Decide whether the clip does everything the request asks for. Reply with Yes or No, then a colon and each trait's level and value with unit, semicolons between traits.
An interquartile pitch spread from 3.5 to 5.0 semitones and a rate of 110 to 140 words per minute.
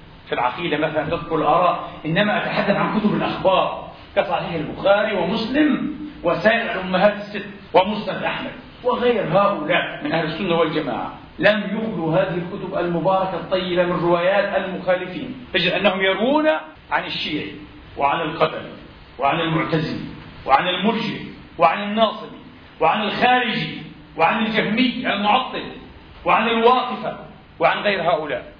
Yes: average, 4.5 semitones; average, 115 wpm